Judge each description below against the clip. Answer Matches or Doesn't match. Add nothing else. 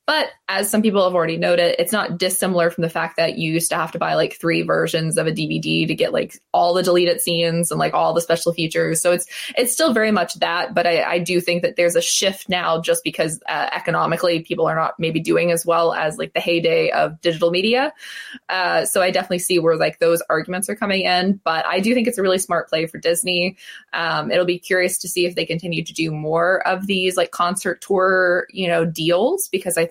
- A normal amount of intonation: Doesn't match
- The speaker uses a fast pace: Matches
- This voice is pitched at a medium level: Matches